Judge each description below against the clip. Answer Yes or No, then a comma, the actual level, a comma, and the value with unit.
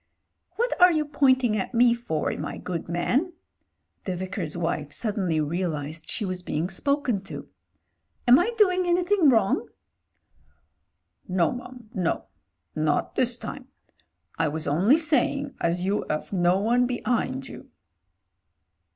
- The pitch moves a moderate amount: No, wide, 7.6 semitones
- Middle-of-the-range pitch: No, high, 210 Hz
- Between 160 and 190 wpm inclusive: No, slow, 135 wpm